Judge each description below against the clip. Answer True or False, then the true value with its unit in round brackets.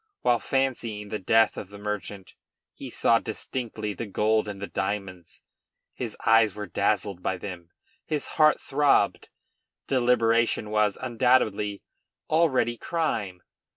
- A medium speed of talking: False (125 wpm)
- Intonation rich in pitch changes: False (3.2 semitones)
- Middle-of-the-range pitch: False (110 Hz)